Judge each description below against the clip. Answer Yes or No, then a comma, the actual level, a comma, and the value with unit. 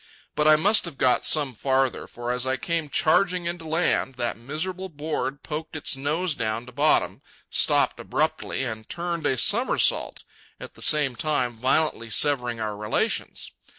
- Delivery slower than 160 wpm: No, average, 165 wpm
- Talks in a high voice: No, medium, 145 Hz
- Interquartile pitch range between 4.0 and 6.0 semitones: Yes, average, 4.6 semitones